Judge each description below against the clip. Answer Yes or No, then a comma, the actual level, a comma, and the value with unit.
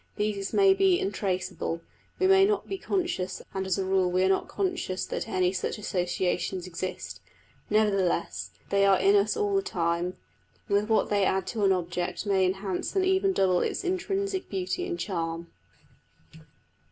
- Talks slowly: No, average, 170 wpm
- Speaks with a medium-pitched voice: No, high, 195 Hz